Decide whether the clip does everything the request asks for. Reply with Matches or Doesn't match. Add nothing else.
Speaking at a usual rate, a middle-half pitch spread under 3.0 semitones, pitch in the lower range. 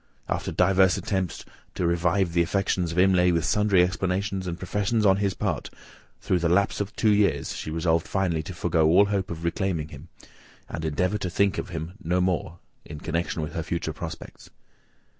Matches